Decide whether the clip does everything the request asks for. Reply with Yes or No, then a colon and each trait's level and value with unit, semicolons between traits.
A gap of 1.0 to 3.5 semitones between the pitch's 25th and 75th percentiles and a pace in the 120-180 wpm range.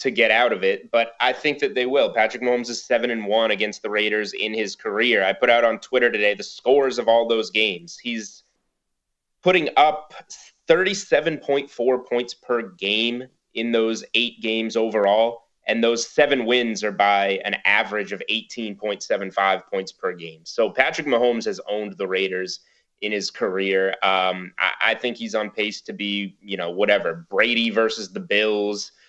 Yes: average, 2.9 semitones; average, 175 wpm